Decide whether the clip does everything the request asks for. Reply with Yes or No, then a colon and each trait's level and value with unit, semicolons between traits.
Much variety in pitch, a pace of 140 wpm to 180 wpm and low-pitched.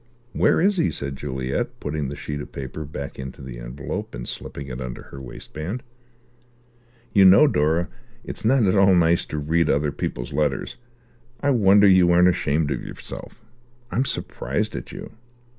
Yes: wide, 5.8 semitones; average, 175 wpm; very low, 75 Hz